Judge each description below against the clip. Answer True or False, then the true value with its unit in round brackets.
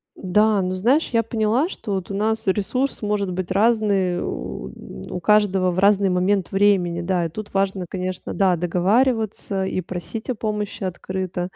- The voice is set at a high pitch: True (195 Hz)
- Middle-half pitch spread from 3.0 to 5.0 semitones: False (2.6 semitones)